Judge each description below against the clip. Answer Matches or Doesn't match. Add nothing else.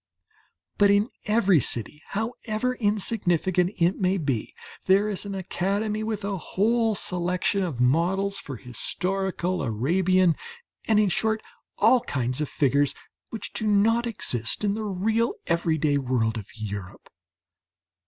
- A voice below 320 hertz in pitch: Matches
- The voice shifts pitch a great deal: Matches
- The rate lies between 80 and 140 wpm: Matches